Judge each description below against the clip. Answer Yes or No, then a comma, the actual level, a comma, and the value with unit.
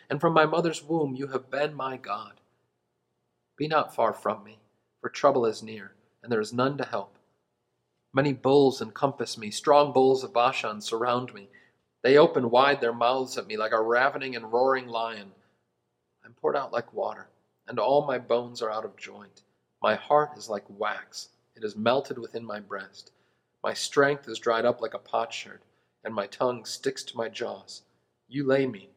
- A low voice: Yes, low, 115 Hz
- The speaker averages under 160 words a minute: No, average, 190 wpm